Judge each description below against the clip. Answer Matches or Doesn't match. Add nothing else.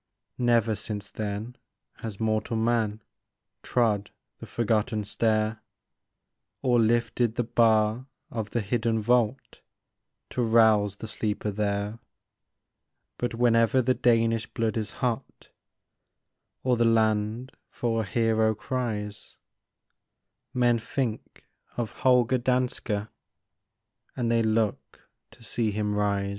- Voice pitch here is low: Matches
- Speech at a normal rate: Doesn't match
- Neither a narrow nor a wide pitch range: Doesn't match